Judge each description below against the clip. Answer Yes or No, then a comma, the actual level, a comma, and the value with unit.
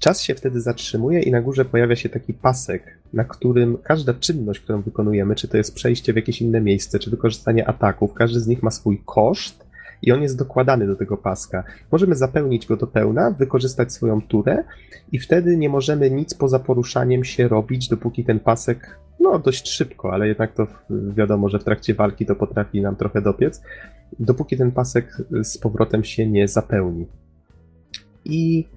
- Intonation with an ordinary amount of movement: Yes, average, 3.5 semitones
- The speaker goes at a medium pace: No, fast, 180 wpm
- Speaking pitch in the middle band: No, low, 115 Hz